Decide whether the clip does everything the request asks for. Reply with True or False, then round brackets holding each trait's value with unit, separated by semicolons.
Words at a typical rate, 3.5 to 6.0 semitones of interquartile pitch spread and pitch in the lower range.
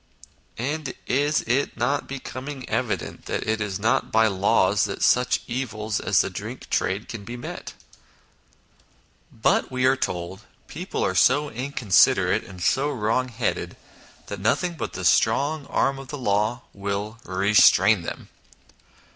True (145 wpm; 4.8 semitones; 115 Hz)